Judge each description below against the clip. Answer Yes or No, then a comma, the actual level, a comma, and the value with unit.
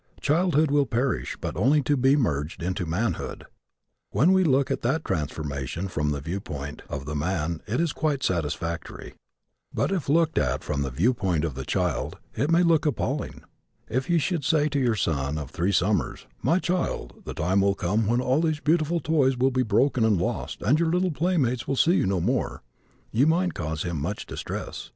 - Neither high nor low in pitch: No, low, 120 Hz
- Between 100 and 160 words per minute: No, average, 195 wpm